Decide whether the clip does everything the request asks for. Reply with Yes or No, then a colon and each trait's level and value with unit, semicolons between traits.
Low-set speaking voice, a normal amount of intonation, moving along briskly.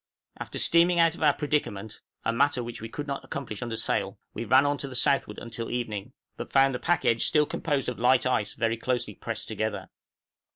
Yes: low, 125 Hz; average, 4.1 semitones; fast, 210 wpm